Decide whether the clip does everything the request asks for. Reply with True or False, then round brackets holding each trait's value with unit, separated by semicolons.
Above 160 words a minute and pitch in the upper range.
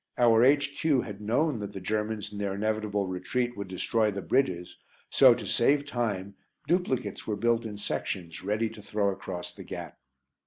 False (170 wpm; 105 Hz)